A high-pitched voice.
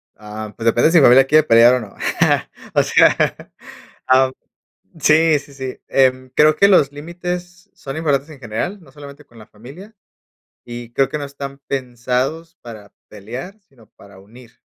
No: low, 135 Hz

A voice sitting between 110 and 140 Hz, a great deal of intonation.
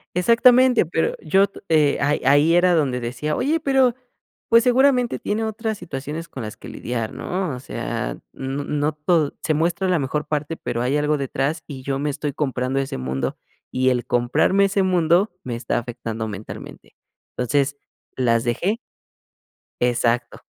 No: medium, 150 Hz; wide, 6.4 semitones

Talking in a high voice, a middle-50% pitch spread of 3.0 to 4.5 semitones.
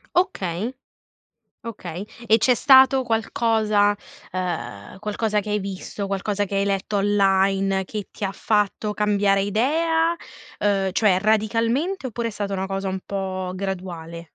No: high, 205 Hz; narrow, 2.5 semitones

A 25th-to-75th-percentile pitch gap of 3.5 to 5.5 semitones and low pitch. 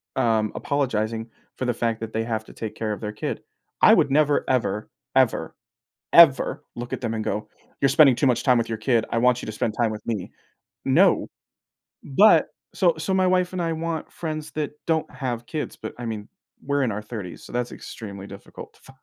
Yes: average, 5.0 semitones; low, 120 Hz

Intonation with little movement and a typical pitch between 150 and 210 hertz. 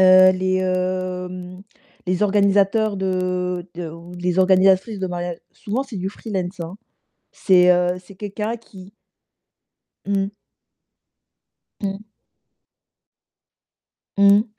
Yes: narrow, 1.7 semitones; medium, 185 Hz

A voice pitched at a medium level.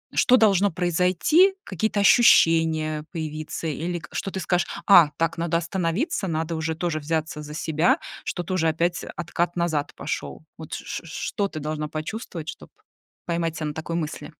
Yes: medium, 165 Hz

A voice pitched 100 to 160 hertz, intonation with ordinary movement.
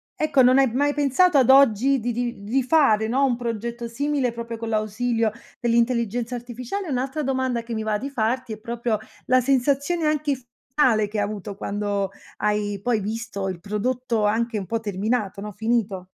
No: high, 235 Hz; average, 3.4 semitones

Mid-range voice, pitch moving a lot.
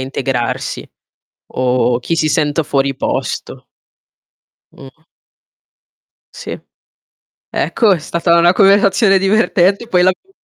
Yes: medium, 170 Hz; wide, 6.0 semitones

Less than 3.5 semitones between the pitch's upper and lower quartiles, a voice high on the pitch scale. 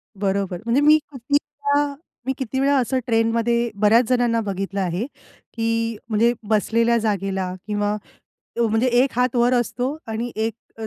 Yes: average, 2.9 semitones; high, 230 Hz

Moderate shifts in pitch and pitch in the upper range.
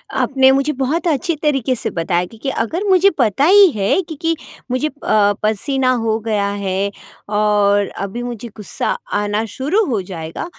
No: wide, 6.0 semitones; high, 235 Hz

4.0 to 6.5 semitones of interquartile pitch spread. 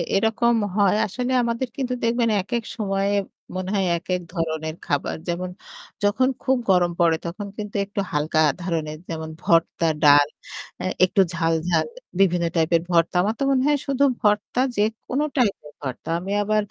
Yes: average, 5.1 semitones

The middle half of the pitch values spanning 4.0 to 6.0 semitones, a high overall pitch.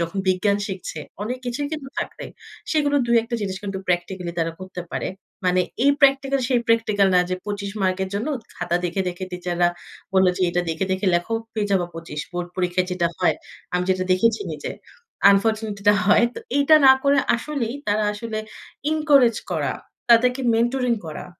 Yes: average, 4.8 semitones; high, 205 Hz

